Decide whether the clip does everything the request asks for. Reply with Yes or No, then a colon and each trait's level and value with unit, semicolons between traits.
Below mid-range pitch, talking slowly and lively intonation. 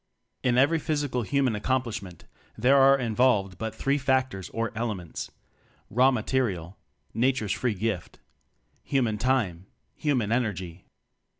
No: low, 120 Hz; slow, 125 wpm; average, 4.1 semitones